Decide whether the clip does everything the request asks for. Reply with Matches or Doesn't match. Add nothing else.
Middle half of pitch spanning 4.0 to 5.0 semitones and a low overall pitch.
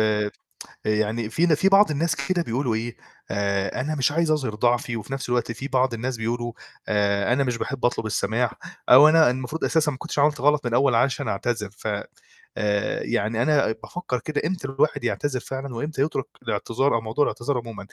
Matches